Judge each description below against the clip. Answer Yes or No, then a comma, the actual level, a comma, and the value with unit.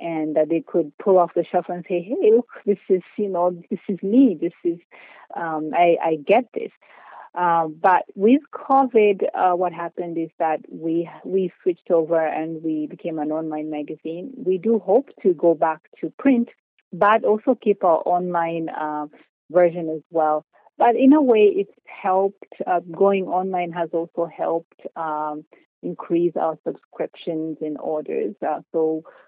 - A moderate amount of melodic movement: Yes, average, 3.5 semitones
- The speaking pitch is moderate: Yes, medium, 175 Hz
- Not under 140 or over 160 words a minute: No, average, 170 wpm